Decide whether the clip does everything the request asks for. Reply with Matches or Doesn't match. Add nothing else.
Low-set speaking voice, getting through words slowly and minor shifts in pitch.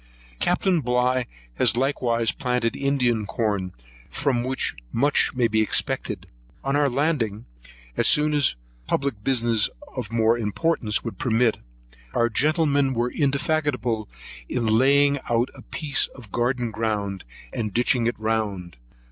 Doesn't match